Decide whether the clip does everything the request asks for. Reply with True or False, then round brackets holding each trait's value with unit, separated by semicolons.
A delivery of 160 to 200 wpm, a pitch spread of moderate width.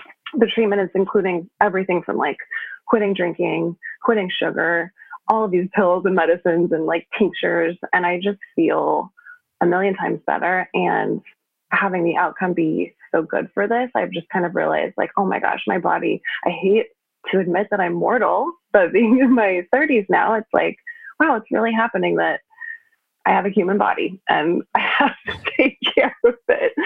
False (180 wpm; 6.9 semitones)